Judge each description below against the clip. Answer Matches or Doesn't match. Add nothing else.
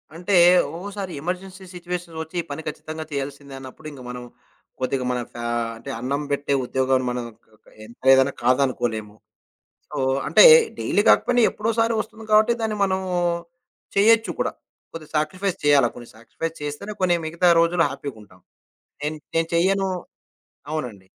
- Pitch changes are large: Matches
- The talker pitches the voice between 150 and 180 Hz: Matches